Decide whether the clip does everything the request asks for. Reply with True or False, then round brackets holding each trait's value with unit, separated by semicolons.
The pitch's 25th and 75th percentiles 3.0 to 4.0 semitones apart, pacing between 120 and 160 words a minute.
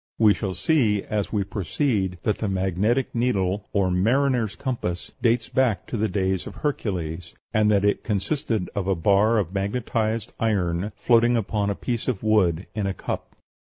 False (3.4 semitones; 170 wpm)